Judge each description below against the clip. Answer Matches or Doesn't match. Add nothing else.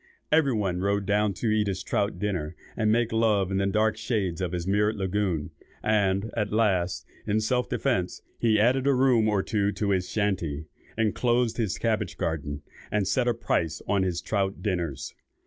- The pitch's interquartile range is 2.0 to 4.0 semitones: Matches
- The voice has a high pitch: Doesn't match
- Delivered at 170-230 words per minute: Matches